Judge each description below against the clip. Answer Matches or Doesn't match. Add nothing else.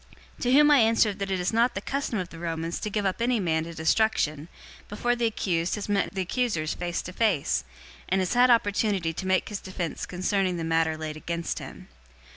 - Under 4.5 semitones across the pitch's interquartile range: Doesn't match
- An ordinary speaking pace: Doesn't match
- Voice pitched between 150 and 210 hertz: Matches